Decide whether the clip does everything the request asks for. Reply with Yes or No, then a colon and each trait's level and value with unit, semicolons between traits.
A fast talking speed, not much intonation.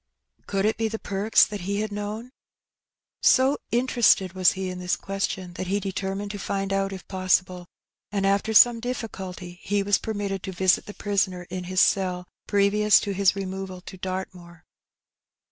No: average, 175 wpm; narrow, 1.7 semitones